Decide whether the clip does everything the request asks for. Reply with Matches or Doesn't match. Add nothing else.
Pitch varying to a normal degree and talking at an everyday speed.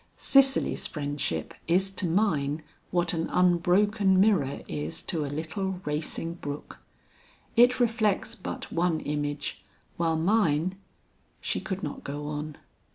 Doesn't match